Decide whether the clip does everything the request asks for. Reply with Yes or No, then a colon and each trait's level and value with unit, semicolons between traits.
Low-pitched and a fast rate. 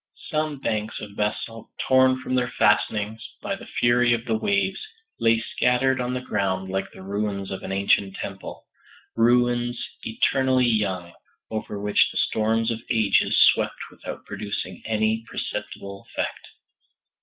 No: low, 110 Hz; average, 145 wpm